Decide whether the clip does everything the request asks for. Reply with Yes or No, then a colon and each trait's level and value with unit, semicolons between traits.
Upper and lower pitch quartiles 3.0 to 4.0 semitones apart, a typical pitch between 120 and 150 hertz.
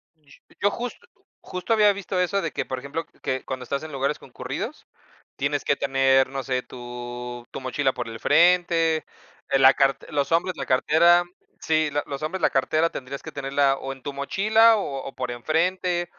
No: average, 4.6 semitones; medium, 140 Hz